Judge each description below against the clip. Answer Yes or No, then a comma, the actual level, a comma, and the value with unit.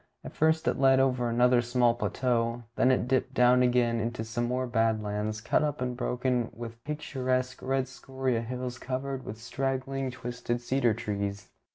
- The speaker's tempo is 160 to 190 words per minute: Yes, average, 170 wpm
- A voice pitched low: Yes, low, 125 Hz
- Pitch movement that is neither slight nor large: No, narrow, 1.8 semitones